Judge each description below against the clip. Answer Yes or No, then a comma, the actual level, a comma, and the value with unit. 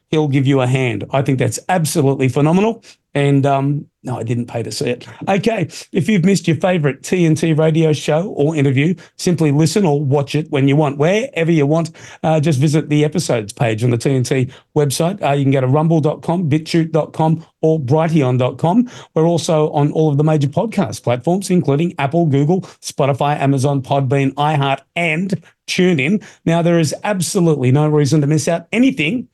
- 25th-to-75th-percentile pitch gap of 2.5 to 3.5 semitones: Yes, average, 3.2 semitones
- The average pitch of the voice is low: No, medium, 155 Hz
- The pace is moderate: Yes, average, 180 wpm